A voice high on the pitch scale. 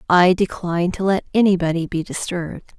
No: medium, 180 Hz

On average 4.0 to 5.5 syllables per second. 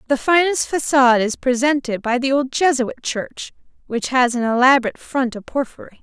Yes: 5.4 syllables/s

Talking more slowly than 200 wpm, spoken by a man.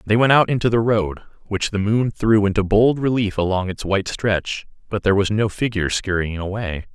No: fast, 205 wpm; male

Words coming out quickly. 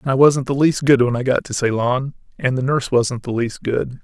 Yes: fast, 265 wpm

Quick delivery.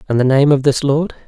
Yes: fast, 285 wpm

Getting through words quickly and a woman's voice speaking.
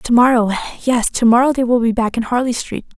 Yes: fast, 220 wpm; female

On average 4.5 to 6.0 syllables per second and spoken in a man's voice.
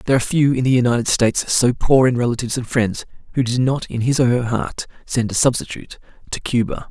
No: 6.3 syllables/s; male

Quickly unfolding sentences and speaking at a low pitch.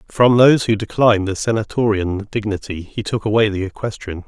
No: average, 170 wpm; low, 105 Hz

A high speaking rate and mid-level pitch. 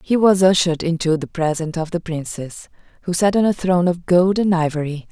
Yes: fast, 210 wpm; medium, 170 Hz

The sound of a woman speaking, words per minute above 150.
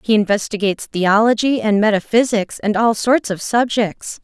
No: female; average, 140 wpm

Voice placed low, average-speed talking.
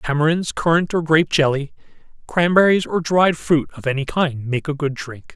No: medium, 155 Hz; average, 180 wpm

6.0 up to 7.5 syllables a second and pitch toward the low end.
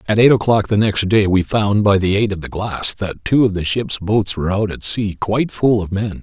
No: 5.1 syllables/s; low, 105 Hz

